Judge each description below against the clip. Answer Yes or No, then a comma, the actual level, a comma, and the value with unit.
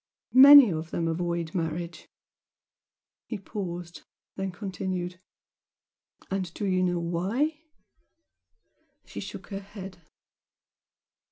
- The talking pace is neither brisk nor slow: No, slow, 100 wpm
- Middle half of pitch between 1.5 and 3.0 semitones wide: Yes, narrow, 2.4 semitones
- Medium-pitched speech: Yes, medium, 180 Hz